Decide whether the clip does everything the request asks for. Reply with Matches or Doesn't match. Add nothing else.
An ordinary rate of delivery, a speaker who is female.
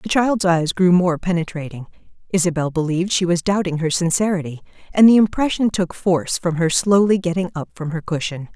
Matches